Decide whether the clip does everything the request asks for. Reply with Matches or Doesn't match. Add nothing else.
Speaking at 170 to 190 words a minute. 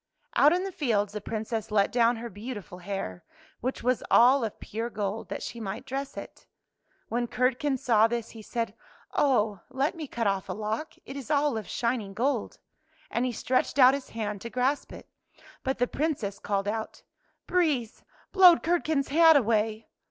Matches